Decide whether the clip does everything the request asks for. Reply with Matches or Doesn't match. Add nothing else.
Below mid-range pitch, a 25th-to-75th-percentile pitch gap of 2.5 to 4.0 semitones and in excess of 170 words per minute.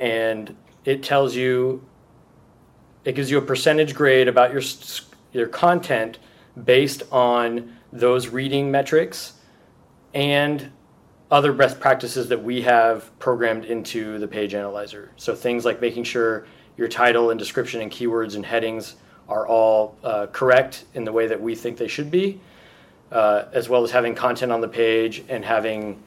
Doesn't match